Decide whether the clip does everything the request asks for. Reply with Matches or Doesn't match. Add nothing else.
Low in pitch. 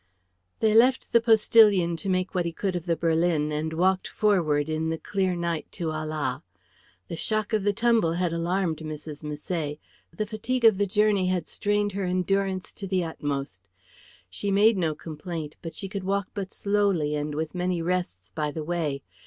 Doesn't match